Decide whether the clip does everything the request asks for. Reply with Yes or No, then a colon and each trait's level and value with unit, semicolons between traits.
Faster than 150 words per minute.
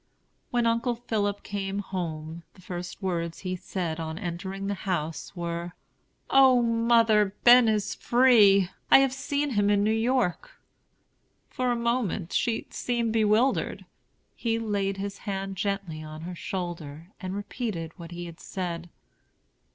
No: average, 145 wpm